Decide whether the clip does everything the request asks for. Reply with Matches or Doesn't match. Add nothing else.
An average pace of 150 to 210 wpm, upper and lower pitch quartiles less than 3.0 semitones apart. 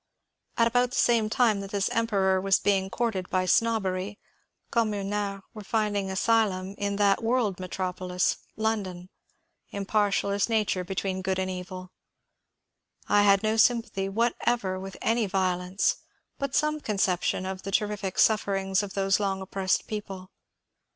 Doesn't match